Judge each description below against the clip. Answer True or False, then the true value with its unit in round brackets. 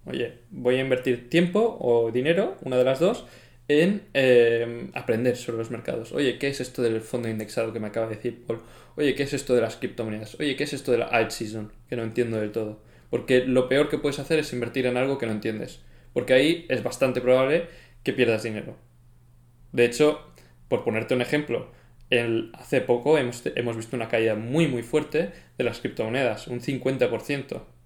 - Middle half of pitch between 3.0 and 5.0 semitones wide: False (2.6 semitones)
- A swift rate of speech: True (200 wpm)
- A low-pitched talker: True (120 Hz)